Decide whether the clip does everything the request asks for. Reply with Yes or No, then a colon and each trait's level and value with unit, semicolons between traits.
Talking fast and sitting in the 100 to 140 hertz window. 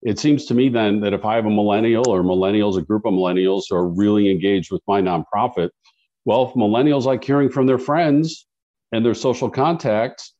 Yes: fast, 210 wpm; low, 110 Hz